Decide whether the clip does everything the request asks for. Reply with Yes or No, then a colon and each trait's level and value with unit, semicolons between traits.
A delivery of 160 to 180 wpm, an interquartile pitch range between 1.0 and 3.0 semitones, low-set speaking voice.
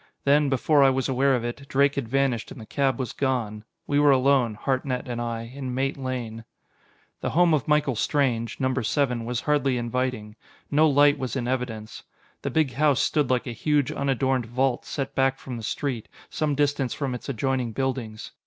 No: average, 190 wpm; narrow, 2.5 semitones; low, 130 Hz